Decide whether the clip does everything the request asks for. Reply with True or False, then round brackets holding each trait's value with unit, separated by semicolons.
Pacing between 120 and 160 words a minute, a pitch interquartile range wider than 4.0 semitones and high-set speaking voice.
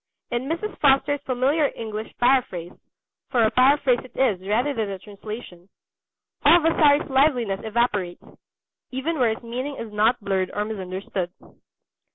True (140 wpm; 4.7 semitones; 240 Hz)